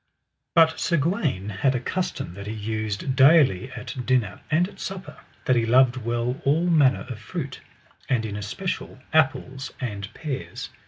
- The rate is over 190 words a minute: No, average, 160 wpm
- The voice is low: Yes, low, 130 Hz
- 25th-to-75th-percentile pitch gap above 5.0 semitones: Yes, wide, 5.6 semitones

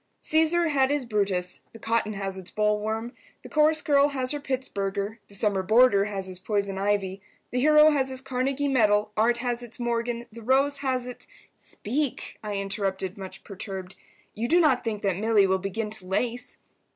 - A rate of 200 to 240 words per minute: No, average, 175 wpm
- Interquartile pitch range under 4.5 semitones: No, average, 4.8 semitones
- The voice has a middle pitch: No, high, 225 Hz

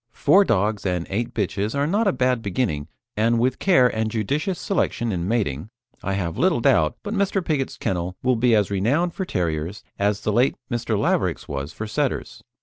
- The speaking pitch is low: Yes, low, 110 Hz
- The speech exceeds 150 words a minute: Yes, average, 190 wpm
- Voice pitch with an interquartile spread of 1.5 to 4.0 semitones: No, average, 5.3 semitones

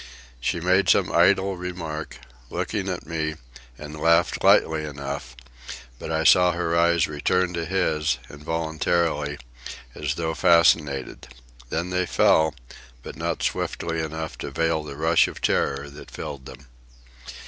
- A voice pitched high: No, very low, 80 Hz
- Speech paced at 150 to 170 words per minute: No, slow, 135 wpm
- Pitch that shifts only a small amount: Yes, narrow, 2.2 semitones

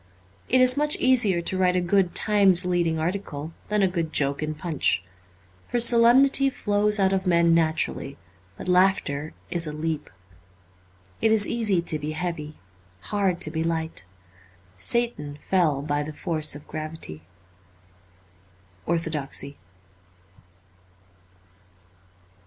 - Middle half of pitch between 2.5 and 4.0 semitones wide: No, average, 4.6 semitones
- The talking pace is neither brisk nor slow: No, slow, 130 wpm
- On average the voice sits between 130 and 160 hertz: No, medium, 170 Hz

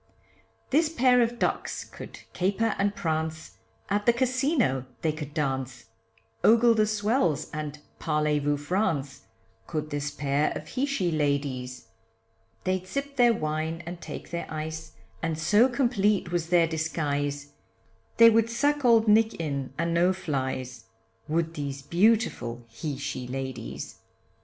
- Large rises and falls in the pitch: Yes, wide, 7.1 semitones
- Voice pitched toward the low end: No, medium, 160 Hz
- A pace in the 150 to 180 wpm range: No, average, 140 wpm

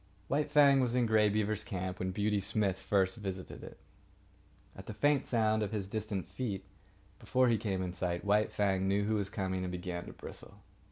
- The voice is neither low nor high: No, low, 100 Hz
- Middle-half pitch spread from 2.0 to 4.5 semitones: Yes, narrow, 2.6 semitones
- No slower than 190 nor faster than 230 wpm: Yes, average, 200 wpm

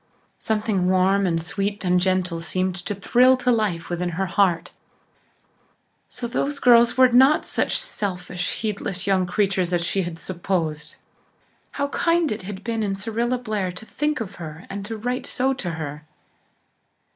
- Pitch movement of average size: Yes, average, 4.6 semitones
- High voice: Yes, high, 195 Hz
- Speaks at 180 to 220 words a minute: No, average, 155 wpm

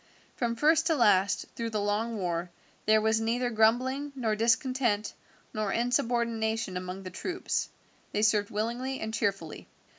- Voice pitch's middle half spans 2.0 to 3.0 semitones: Yes, average, 2.7 semitones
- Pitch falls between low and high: No, high, 225 Hz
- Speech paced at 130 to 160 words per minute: Yes, average, 145 wpm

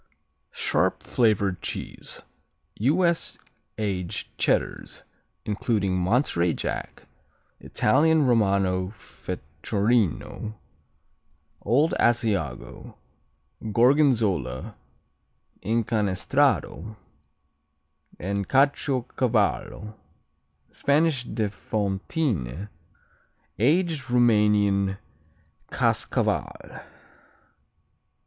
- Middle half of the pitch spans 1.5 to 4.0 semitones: No, average, 4.7 semitones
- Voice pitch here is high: No, low, 110 Hz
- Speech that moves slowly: Yes, slow, 50 wpm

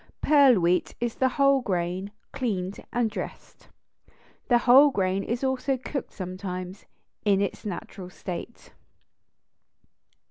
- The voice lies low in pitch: No, high, 210 Hz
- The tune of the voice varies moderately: No, wide, 5.8 semitones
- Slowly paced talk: Yes, slow, 115 wpm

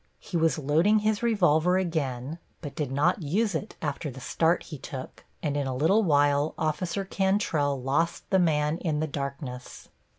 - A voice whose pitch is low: No, medium, 155 Hz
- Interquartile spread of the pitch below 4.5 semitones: Yes, average, 3.9 semitones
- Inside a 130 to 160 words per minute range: No, average, 170 wpm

